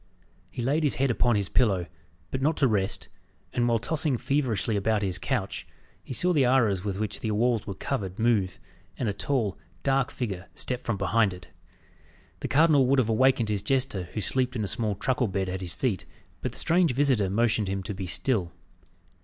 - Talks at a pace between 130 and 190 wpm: No, average, 200 wpm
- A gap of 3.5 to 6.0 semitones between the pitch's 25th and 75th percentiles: Yes, average, 5.0 semitones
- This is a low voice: Yes, low, 115 Hz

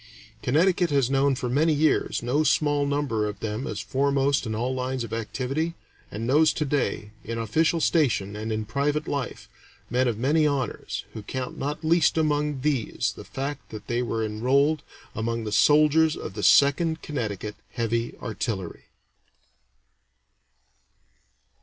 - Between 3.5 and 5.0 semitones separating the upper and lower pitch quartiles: Yes, average, 4.5 semitones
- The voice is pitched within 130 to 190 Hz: Yes, low, 135 Hz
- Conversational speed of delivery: Yes, average, 150 wpm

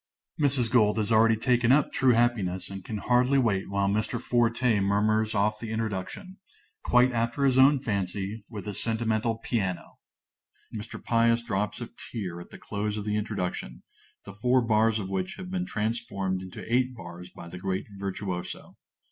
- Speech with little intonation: No, average, 3.4 semitones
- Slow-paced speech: No, average, 170 wpm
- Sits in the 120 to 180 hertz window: No, low, 110 Hz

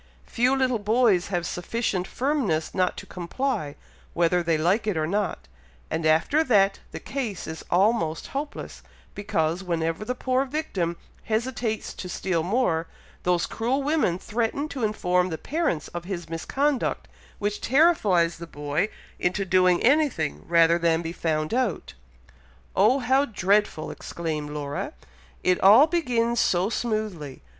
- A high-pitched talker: Yes, high, 195 Hz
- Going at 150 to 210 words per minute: No, average, 140 wpm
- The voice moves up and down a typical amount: No, wide, 6.3 semitones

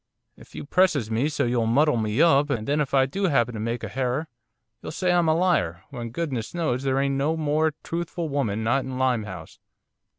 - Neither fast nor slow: No, fast, 220 wpm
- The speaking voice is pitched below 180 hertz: Yes, low, 135 Hz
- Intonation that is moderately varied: Yes, average, 4.9 semitones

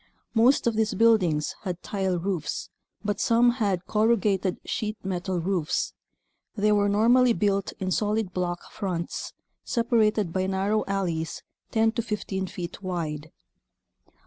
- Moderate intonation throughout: Yes, average, 3.3 semitones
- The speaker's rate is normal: No, slow, 130 wpm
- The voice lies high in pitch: Yes, high, 200 Hz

